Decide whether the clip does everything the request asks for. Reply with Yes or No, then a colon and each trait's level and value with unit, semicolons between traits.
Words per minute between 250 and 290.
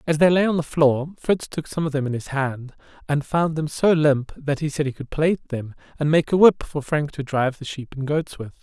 Yes: fast, 270 wpm